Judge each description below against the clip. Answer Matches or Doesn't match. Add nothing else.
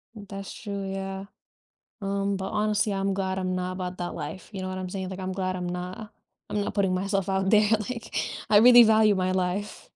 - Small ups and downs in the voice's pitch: Matches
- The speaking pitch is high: Matches